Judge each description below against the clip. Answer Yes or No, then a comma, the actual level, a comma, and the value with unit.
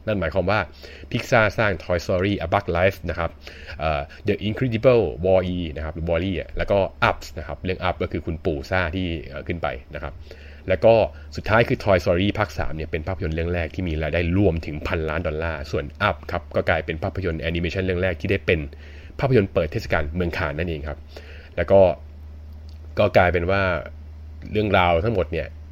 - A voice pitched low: Yes, very low, 85 Hz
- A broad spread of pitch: No, average, 3.7 semitones